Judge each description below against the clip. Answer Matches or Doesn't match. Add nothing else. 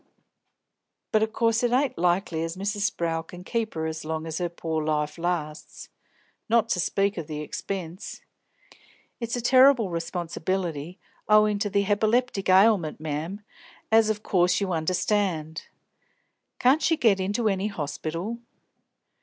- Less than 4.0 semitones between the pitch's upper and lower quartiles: Doesn't match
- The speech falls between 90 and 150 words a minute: Matches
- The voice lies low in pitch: Doesn't match